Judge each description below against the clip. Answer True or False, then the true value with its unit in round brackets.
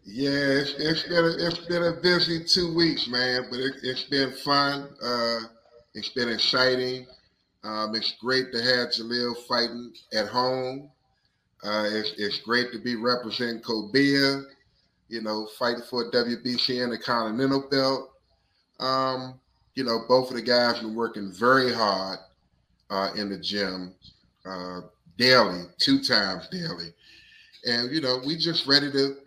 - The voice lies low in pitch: True (125 Hz)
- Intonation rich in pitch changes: False (3.7 semitones)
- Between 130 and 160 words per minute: True (150 wpm)